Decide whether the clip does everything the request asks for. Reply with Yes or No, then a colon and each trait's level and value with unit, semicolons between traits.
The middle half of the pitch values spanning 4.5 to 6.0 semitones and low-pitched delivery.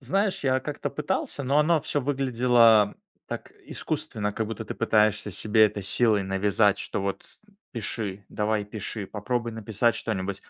No: average, 3.6 semitones; low, 110 Hz